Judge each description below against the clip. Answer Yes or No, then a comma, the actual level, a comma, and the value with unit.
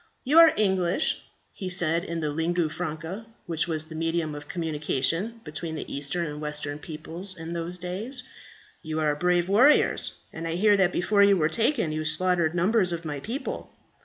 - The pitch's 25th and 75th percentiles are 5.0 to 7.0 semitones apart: No, average, 3.3 semitones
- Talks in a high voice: No, medium, 170 Hz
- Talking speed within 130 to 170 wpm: No, average, 180 wpm